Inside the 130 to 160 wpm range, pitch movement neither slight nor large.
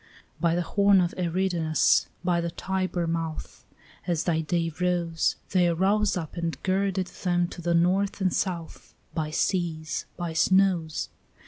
No: average, 145 wpm; narrow, 2.1 semitones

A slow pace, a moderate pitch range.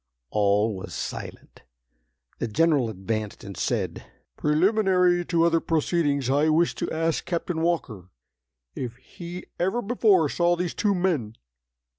No: slow, 130 wpm; wide, 7.0 semitones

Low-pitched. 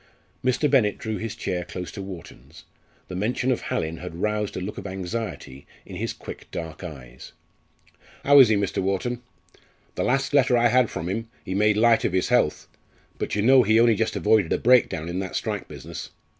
Yes: low, 105 Hz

